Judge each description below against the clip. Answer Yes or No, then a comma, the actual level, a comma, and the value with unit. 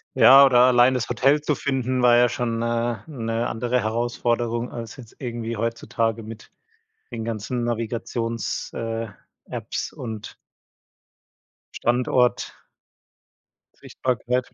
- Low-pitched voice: Yes, low, 120 Hz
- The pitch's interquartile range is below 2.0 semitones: Yes, narrow, 1.4 semitones